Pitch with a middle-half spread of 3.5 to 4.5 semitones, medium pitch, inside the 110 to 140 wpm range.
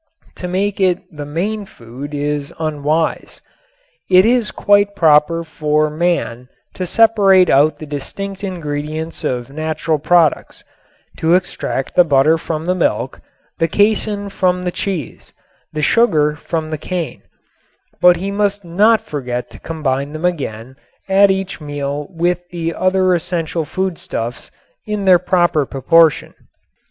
Yes: average, 4.0 semitones; medium, 165 Hz; slow, 135 wpm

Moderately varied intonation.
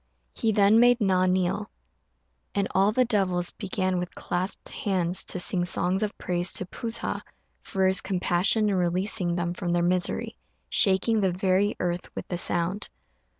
No: narrow, 2.2 semitones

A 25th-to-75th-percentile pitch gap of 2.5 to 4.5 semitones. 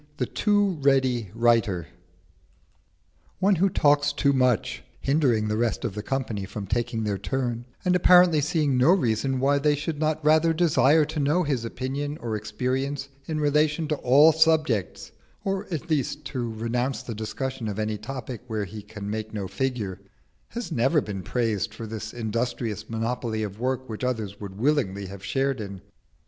No: average, 5.3 semitones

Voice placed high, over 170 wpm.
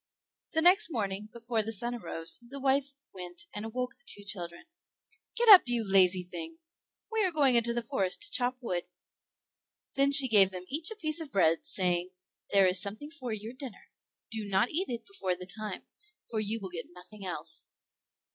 Yes: high, 225 Hz; average, 190 wpm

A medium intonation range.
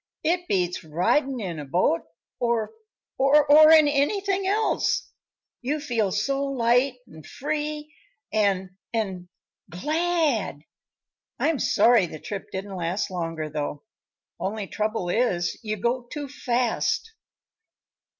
No: wide, 8.0 semitones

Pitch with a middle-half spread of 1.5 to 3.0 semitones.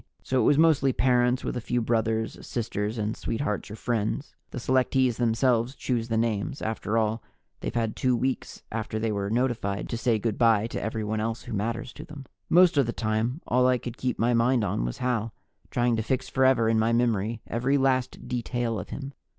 Yes: narrow, 2.4 semitones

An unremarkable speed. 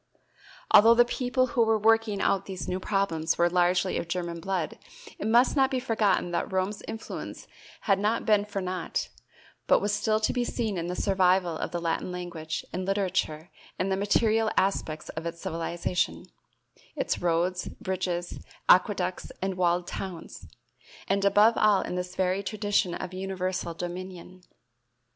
Yes: average, 160 wpm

